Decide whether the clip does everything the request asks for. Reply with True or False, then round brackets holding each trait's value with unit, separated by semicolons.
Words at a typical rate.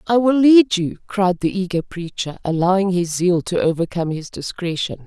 True (180 wpm)